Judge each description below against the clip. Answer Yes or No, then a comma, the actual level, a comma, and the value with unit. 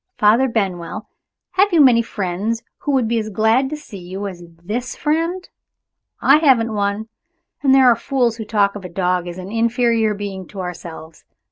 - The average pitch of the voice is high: Yes, high, 220 Hz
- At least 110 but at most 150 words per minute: No, average, 180 wpm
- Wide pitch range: No, average, 4.6 semitones